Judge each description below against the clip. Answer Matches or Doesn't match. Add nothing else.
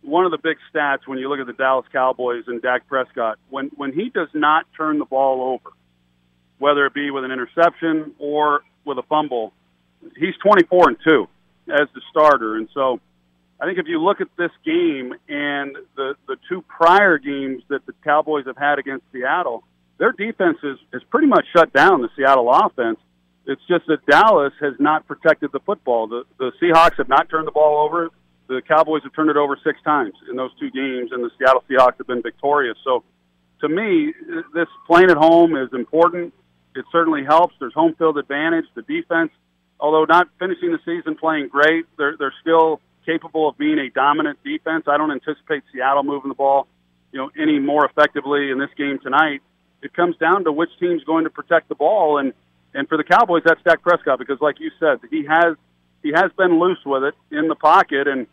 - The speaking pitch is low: Doesn't match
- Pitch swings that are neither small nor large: Matches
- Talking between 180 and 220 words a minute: Matches